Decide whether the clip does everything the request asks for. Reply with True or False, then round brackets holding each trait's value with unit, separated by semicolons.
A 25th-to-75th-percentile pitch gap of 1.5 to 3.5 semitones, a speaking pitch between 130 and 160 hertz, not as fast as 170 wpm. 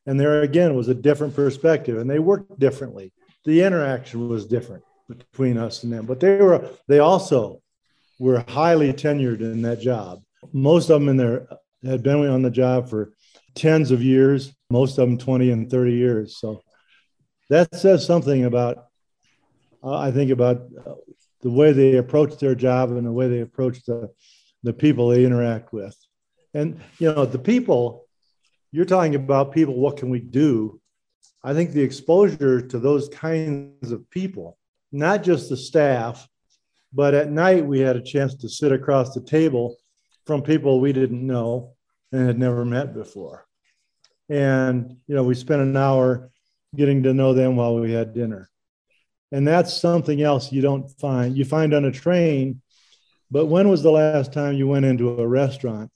False (3.2 semitones; 135 Hz; 175 wpm)